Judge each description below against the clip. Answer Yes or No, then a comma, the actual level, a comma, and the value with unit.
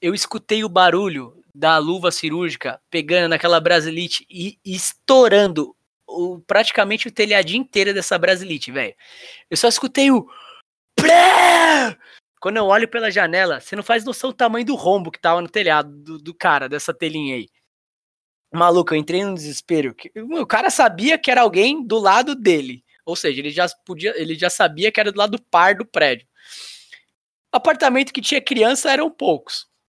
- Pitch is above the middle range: Yes, high, 195 Hz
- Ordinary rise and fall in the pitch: No, wide, 6.2 semitones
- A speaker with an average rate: Yes, average, 165 wpm